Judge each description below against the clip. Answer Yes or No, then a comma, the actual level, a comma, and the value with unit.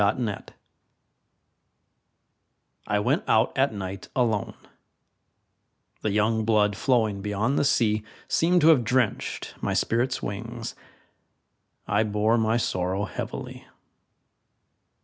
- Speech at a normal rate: No, slow, 110 wpm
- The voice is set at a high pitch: No, low, 110 Hz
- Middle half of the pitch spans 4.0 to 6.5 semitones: No, average, 2.7 semitones